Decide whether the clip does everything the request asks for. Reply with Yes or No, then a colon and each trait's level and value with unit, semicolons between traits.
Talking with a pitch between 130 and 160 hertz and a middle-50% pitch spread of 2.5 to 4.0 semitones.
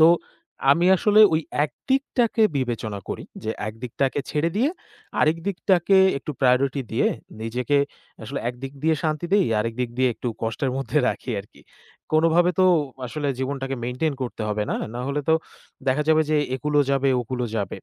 No: medium, 140 Hz; average, 4.4 semitones